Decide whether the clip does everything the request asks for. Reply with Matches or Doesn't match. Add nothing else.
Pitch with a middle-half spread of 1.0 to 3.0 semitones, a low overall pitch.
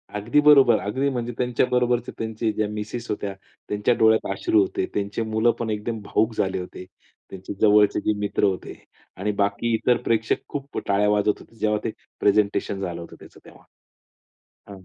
Matches